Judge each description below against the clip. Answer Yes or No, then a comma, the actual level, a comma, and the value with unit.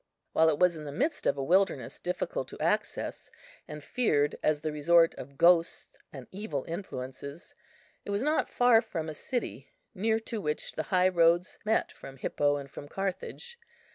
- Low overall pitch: No, medium, 170 Hz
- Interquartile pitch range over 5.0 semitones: Yes, wide, 5.5 semitones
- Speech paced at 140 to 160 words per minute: No, average, 175 wpm